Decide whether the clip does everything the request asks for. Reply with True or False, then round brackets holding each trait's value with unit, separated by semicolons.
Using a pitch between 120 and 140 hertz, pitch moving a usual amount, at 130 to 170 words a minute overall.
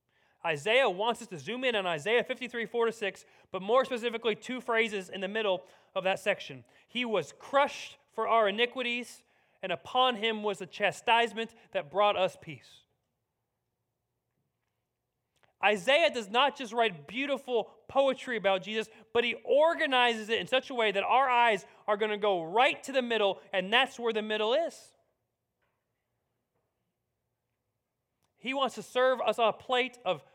False (220 Hz; 4.7 semitones; 160 wpm)